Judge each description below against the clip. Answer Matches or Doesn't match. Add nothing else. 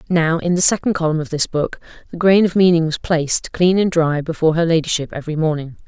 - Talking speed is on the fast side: Matches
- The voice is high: Doesn't match